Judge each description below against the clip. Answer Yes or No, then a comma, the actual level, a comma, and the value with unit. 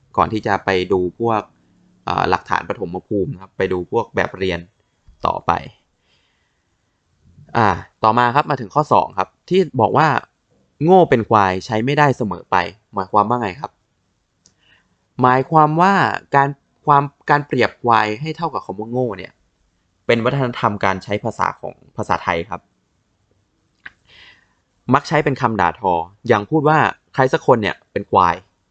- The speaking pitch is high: No, low, 110 Hz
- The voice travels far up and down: Yes, wide, 6.4 semitones